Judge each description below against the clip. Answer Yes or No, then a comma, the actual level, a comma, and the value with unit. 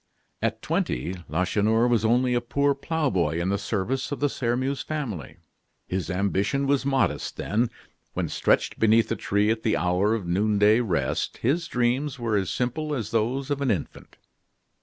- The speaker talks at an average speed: Yes, average, 165 wpm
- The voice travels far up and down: No, average, 4.9 semitones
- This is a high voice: No, low, 115 Hz